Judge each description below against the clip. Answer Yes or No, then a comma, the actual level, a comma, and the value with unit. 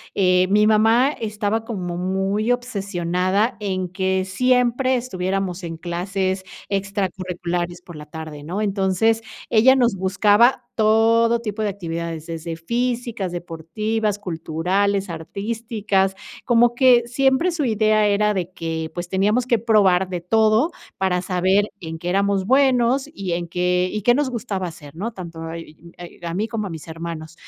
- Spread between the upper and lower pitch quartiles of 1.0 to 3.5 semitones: No, average, 4.0 semitones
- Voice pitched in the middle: No, high, 195 Hz